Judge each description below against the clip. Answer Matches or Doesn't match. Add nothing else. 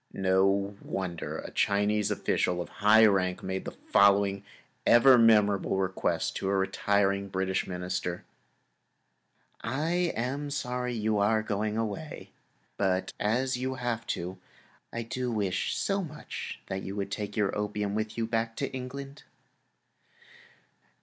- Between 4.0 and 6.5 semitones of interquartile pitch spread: Doesn't match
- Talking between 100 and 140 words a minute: Matches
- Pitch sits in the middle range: Doesn't match